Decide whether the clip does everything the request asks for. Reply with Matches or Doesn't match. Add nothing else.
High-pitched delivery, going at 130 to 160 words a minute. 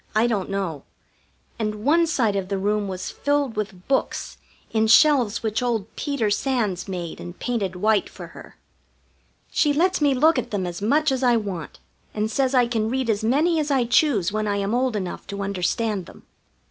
Doesn't match